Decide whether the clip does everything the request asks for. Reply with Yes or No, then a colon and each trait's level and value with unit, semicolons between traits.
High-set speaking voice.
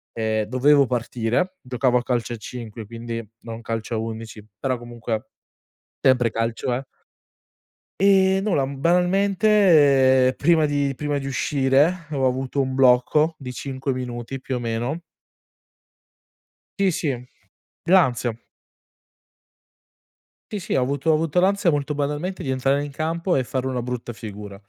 No: low, 130 Hz